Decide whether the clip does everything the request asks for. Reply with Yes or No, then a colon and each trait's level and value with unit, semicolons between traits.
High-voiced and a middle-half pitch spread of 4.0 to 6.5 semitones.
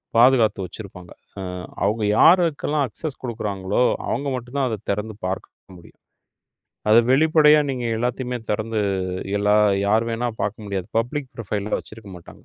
No: low, 115 Hz; average, 4.3 semitones